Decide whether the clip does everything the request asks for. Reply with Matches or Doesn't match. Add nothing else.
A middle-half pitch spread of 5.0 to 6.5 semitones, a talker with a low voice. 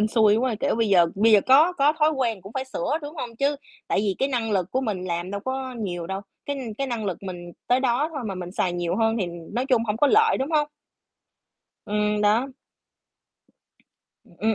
Doesn't match